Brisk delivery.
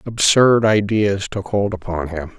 No: average, 150 wpm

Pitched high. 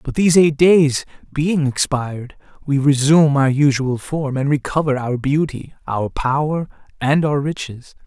No: medium, 140 Hz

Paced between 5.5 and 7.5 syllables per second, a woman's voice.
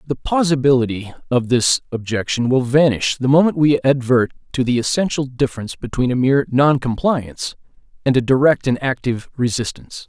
No: 5.7 syllables/s; male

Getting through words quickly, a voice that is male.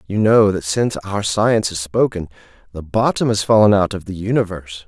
No: average, 195 wpm; male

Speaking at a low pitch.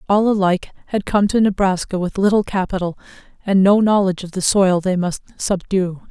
No: high, 190 Hz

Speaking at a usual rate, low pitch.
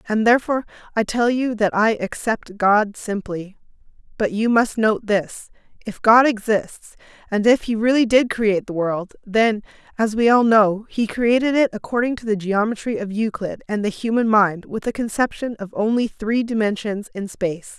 No: average, 180 wpm; high, 220 Hz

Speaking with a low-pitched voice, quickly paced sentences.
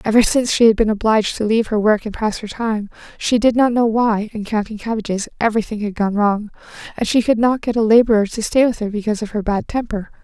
No: high, 220 Hz; fast, 245 wpm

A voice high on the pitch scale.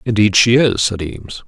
No: low, 105 Hz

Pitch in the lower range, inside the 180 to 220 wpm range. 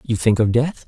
No: low, 120 Hz; fast, 275 wpm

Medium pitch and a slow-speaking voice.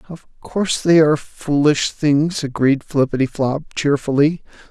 Yes: medium, 145 Hz; slow, 115 wpm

